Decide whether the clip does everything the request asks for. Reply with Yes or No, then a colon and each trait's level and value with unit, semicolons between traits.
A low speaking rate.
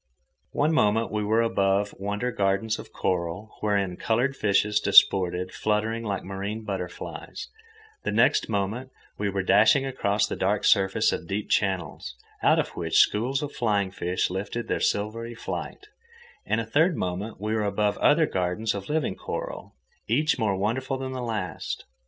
No: average, 160 wpm